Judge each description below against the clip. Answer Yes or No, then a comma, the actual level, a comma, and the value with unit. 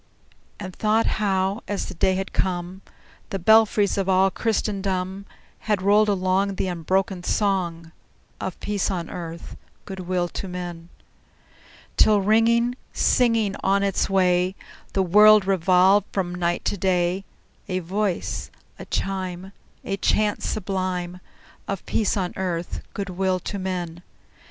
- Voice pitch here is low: No, high, 190 Hz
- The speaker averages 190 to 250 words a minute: No, slow, 135 wpm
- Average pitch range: No, narrow, 1.9 semitones